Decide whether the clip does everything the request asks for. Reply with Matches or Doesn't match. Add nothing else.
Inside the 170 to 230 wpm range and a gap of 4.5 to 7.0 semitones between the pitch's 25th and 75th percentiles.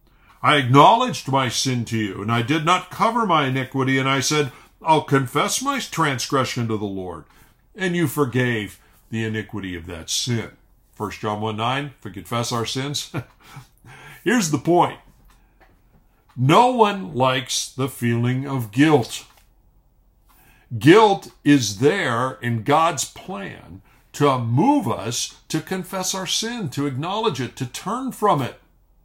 Doesn't match